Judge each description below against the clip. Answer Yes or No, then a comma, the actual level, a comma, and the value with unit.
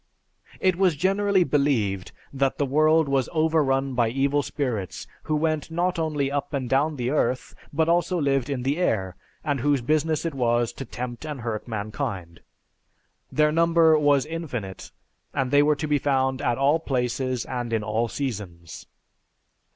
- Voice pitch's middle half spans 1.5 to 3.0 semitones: No, average, 4.2 semitones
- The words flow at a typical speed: Yes, average, 165 wpm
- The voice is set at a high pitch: No, medium, 140 Hz